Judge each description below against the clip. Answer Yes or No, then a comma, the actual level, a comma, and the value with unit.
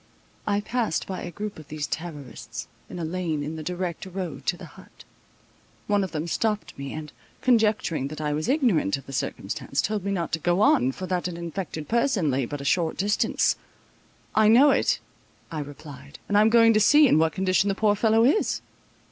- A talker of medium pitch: Yes, medium, 180 Hz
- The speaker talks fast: Yes, fast, 210 wpm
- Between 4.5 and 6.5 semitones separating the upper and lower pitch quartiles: Yes, wide, 5.4 semitones